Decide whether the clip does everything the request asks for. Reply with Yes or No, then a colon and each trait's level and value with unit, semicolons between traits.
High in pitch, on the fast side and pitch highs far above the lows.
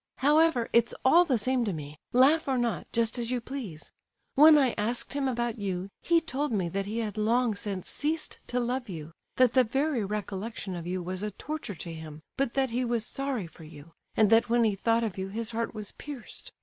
No: high, 230 Hz; fast, 220 wpm; average, 4.7 semitones